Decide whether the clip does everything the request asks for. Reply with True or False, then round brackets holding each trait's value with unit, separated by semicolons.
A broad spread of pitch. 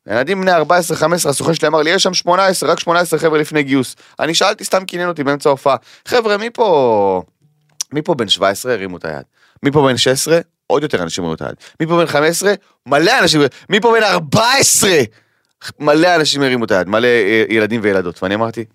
True (7.3 semitones)